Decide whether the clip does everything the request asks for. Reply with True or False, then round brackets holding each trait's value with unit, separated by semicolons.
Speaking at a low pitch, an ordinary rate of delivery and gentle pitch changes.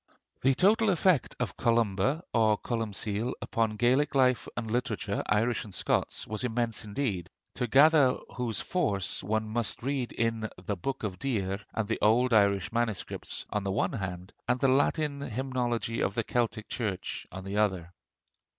False (115 Hz; 160 wpm; 3.6 semitones)